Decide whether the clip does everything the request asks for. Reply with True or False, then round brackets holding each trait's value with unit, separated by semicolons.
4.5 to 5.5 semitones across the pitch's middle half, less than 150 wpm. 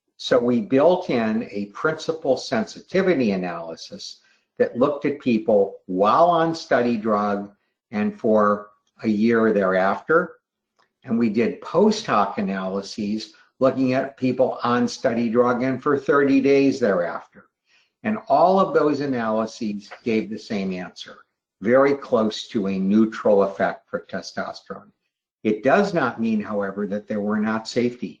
True (5.2 semitones; 140 wpm)